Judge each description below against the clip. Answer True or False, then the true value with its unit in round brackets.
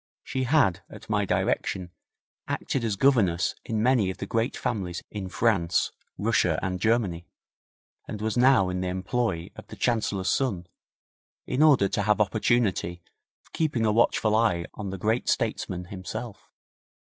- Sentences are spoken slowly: False (155 wpm)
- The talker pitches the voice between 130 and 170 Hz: False (105 Hz)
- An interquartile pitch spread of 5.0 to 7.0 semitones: False (4.2 semitones)